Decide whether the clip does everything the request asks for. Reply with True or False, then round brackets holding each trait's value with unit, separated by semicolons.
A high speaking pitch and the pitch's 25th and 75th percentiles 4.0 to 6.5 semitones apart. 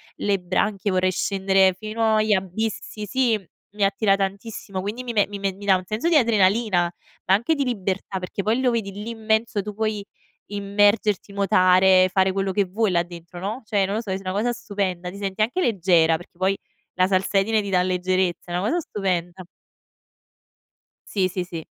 False (195 Hz; 2.5 semitones)